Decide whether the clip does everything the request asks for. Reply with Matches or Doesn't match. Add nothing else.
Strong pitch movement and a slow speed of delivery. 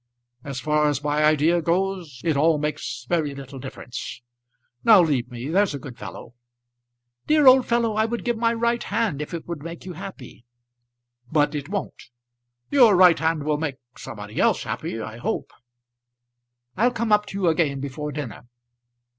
Doesn't match